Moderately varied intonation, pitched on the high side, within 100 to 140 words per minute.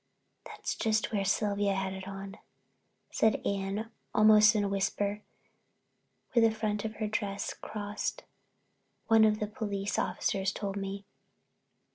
No: narrow, 1.5 semitones; high, 205 Hz; slow, 135 wpm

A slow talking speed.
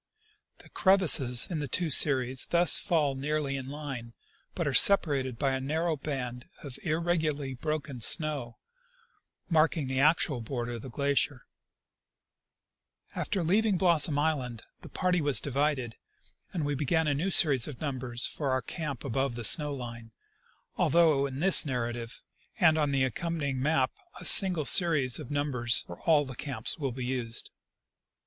No: average, 155 wpm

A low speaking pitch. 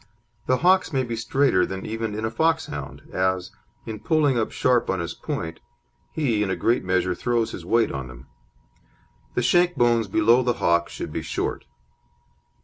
Yes: low, 115 Hz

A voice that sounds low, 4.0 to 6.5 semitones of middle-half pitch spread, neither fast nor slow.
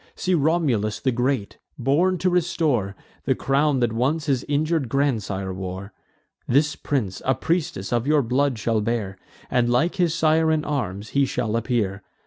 Yes: low, 130 Hz; wide, 5.6 semitones; average, 160 wpm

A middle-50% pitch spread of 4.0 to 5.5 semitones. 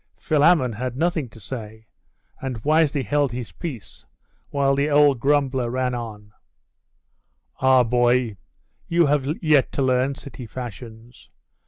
No: average, 3.3 semitones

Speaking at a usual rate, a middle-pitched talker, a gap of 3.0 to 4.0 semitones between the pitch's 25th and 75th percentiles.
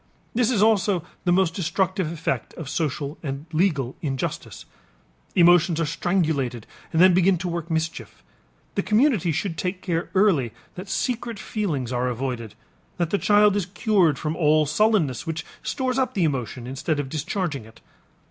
No: average, 160 wpm; medium, 170 Hz; average, 5.0 semitones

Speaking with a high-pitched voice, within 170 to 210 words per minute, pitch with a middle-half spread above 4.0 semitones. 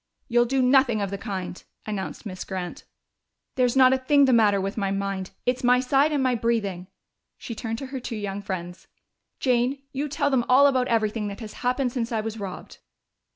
Yes: high, 235 Hz; average, 200 wpm; average, 4.4 semitones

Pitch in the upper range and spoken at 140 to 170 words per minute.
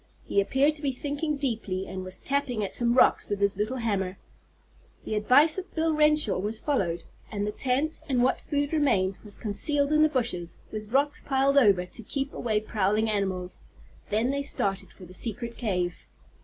No: high, 230 Hz; average, 185 wpm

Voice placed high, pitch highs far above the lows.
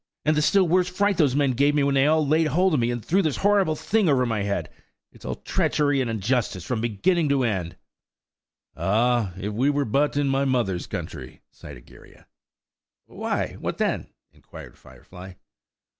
No: low, 135 Hz; wide, 5.9 semitones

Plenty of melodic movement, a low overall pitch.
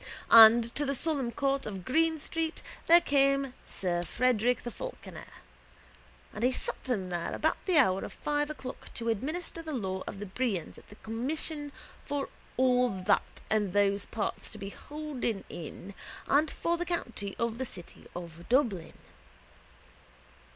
No: wide, 6.4 semitones; high, 245 Hz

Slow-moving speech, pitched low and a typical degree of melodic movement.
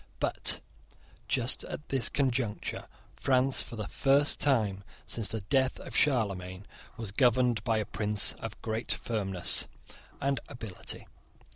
Yes: slow, 130 wpm; low, 115 Hz; average, 4.1 semitones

